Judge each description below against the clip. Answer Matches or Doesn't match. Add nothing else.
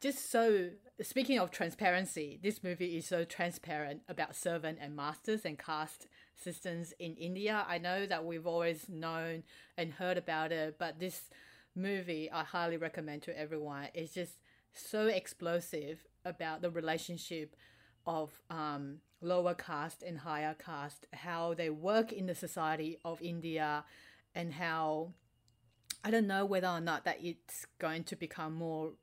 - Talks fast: Doesn't match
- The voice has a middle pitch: Matches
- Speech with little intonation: Matches